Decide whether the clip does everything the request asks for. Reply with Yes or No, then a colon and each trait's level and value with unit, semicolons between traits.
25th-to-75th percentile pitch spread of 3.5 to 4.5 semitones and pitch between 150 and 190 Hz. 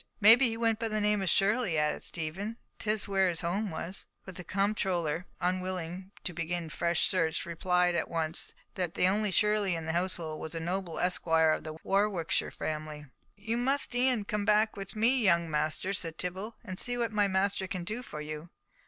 Yes: average, 4.0 semitones; medium, 185 Hz